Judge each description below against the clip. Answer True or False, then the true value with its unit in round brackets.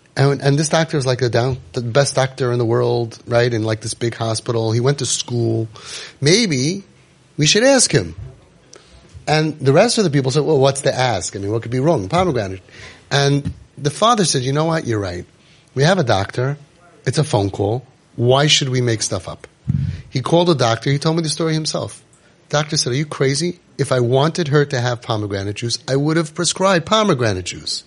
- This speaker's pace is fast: True (210 wpm)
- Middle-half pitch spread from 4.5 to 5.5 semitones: True (4.9 semitones)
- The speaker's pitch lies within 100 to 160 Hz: True (135 Hz)